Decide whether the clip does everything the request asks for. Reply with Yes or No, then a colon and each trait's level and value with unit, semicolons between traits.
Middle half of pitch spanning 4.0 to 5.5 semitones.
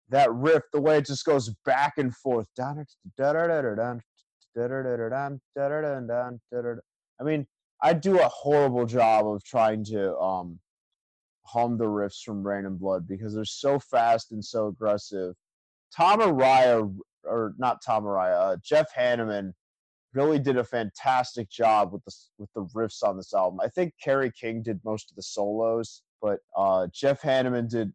Yes: average, 4.7 semitones